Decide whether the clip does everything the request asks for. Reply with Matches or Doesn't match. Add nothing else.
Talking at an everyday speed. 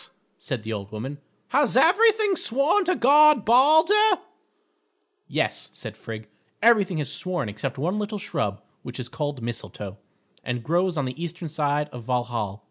Matches